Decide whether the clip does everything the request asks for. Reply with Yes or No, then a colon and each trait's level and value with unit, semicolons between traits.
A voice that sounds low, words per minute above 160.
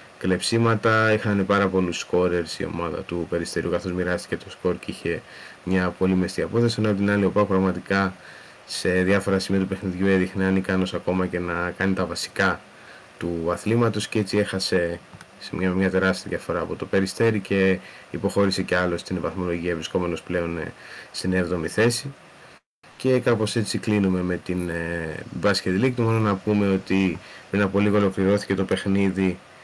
Yes: very low, 95 Hz; fast, 170 wpm